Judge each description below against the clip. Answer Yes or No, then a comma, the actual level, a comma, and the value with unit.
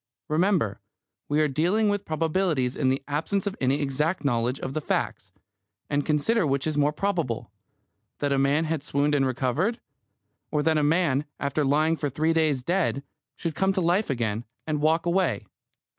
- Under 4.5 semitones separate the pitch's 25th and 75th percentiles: Yes, average, 3.4 semitones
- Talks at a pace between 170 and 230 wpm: Yes, average, 175 wpm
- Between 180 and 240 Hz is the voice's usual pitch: No, medium, 150 Hz